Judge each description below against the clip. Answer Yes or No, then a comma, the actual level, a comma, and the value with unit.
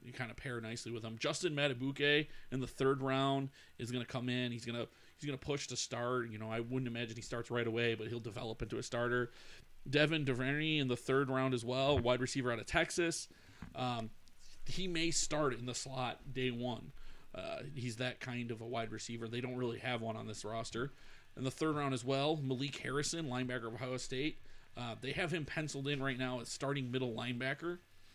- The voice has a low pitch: Yes, low, 125 Hz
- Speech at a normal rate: No, fast, 220 wpm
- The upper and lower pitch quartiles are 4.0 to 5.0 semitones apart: No, narrow, 2.6 semitones